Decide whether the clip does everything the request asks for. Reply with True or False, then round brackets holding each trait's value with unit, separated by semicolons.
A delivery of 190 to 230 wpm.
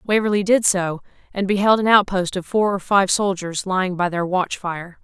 True (205 wpm)